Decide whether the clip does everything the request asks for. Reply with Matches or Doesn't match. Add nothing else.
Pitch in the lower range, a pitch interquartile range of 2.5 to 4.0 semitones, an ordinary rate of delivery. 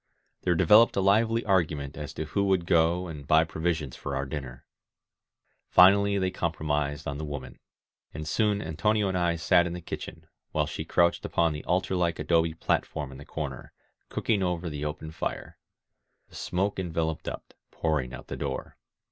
Matches